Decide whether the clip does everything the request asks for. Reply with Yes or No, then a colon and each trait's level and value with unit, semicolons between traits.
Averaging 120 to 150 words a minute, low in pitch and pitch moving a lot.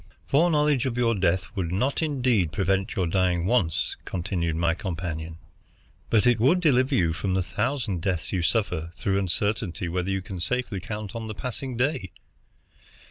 No: average, 165 wpm; very low, 95 Hz; wide, 5.7 semitones